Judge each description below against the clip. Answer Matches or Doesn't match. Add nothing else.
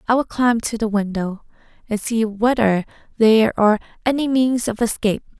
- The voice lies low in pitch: Doesn't match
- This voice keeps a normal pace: Matches